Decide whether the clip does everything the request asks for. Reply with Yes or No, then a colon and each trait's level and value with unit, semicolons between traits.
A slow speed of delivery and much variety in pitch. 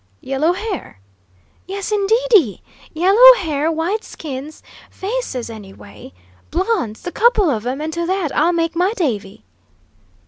Yes: slow, 130 wpm; wide, 6.8 semitones